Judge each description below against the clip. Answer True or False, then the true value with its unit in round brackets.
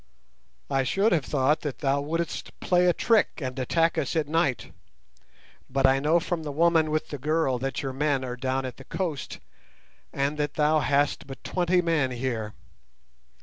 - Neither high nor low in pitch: True (145 Hz)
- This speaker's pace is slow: False (180 wpm)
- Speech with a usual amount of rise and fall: True (3.6 semitones)